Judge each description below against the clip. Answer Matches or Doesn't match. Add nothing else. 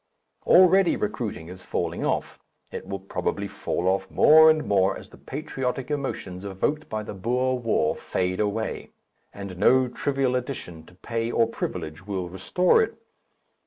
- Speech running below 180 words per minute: Matches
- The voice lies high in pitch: Doesn't match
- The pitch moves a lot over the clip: Matches